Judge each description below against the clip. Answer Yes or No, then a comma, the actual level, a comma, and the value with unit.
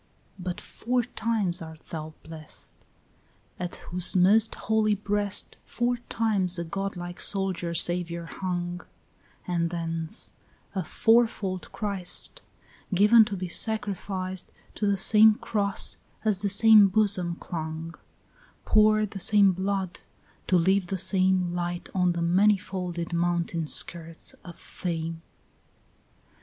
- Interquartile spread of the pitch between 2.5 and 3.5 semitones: Yes, average, 3.1 semitones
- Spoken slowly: Yes, slow, 125 wpm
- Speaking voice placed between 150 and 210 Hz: Yes, medium, 185 Hz